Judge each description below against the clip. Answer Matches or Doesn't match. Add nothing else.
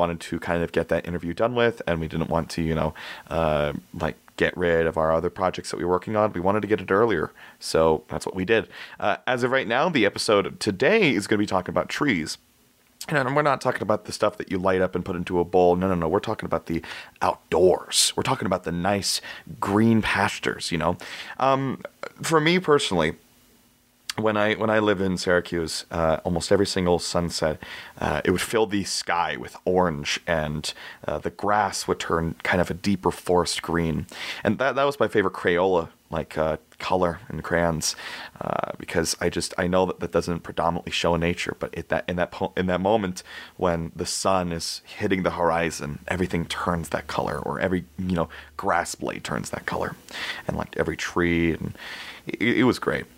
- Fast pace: Matches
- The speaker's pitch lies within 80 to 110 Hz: Matches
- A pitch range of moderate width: Matches